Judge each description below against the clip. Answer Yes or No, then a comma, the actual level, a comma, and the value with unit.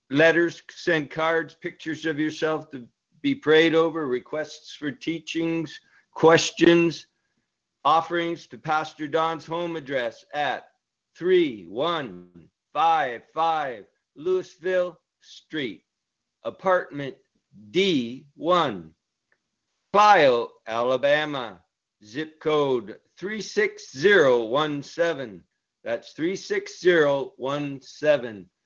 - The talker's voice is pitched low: No, medium, 165 Hz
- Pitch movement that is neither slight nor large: Yes, average, 3.8 semitones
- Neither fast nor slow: No, slow, 70 wpm